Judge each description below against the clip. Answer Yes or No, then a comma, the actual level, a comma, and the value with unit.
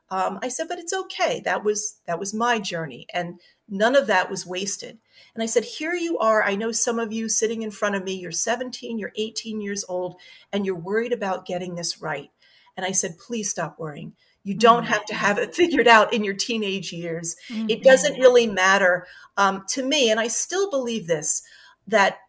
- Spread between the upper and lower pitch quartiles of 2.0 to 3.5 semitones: No, average, 3.9 semitones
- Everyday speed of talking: No, fast, 210 wpm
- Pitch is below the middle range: No, high, 215 Hz